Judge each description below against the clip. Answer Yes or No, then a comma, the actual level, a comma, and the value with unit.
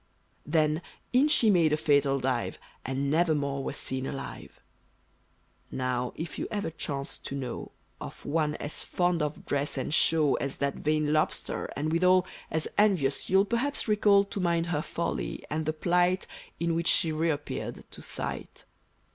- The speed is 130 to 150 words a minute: No, average, 165 wpm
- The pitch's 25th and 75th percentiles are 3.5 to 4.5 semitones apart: Yes, average, 3.8 semitones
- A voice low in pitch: No, medium, 155 Hz